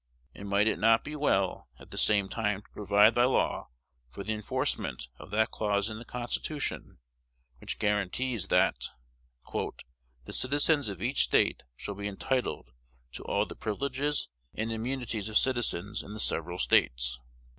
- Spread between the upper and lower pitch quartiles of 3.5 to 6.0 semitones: Yes, average, 3.9 semitones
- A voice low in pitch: Yes, low, 105 Hz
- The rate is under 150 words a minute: No, average, 155 wpm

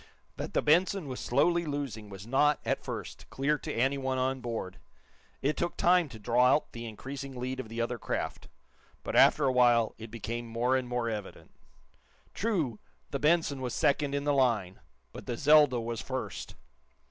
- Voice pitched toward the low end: Yes, low, 130 Hz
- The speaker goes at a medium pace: Yes, average, 180 wpm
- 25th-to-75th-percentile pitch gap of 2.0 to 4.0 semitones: Yes, average, 3.6 semitones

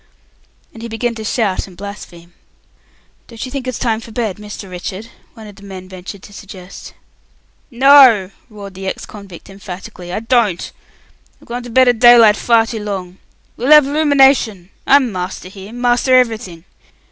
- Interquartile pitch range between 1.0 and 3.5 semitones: No, average, 4.2 semitones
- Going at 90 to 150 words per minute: No, average, 170 wpm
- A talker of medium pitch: No, high, 215 Hz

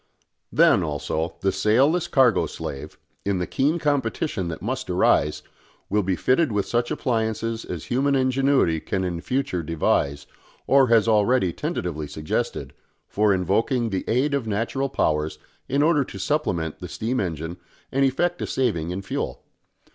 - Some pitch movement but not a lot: No, wide, 6.8 semitones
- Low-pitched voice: Yes, low, 110 Hz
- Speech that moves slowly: No, average, 155 wpm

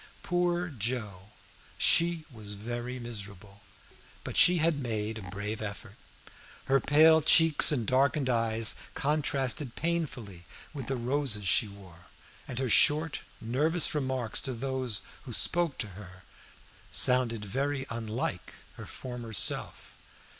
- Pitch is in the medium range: No, low, 125 Hz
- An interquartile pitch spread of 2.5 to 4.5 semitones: No, wide, 5.4 semitones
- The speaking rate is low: Yes, slow, 125 wpm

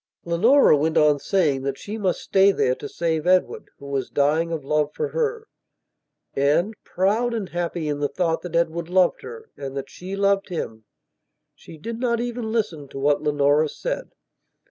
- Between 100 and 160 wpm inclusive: No, average, 180 wpm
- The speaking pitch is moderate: Yes, medium, 170 Hz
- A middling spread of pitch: No, wide, 6.0 semitones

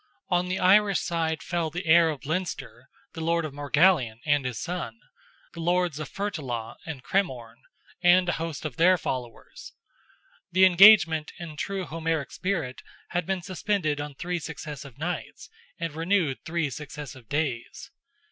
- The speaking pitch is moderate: Yes, medium, 160 Hz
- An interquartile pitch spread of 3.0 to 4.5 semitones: Yes, average, 3.8 semitones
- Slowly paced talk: No, average, 150 wpm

